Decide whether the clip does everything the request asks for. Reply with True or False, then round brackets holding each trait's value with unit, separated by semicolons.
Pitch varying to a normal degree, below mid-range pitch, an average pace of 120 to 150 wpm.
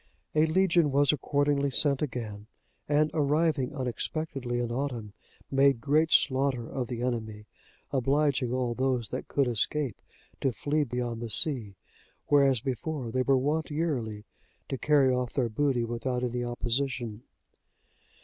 True (3.3 semitones; 130 Hz; 140 wpm)